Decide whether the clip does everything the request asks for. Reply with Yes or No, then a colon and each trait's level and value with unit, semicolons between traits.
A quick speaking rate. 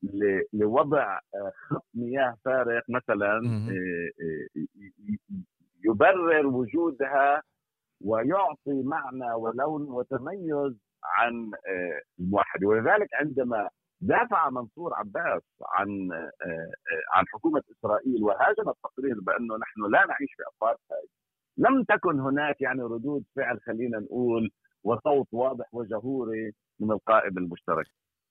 No: average, 95 wpm